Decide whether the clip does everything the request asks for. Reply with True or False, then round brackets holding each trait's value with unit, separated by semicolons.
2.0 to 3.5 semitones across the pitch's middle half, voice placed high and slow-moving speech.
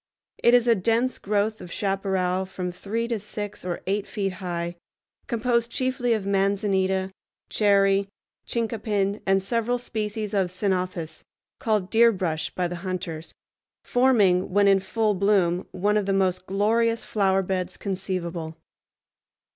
True (2.9 semitones; 195 Hz; 130 wpm)